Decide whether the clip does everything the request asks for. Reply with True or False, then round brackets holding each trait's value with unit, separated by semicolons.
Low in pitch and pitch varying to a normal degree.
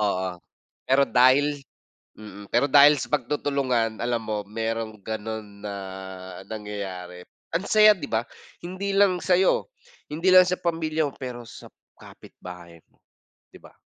False (120 Hz; 6.2 semitones)